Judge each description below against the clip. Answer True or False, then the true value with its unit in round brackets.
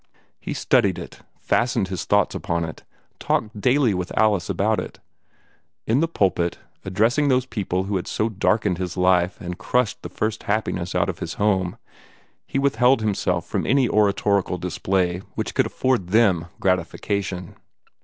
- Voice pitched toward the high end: False (100 Hz)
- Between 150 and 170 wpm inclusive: True (155 wpm)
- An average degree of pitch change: True (3.5 semitones)